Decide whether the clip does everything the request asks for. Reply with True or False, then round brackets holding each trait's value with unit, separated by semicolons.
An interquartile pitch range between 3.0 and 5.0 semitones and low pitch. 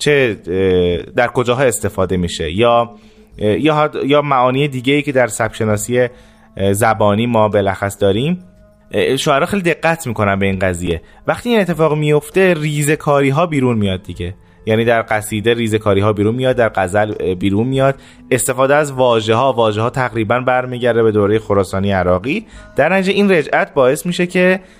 False (5.6 semitones; 115 Hz)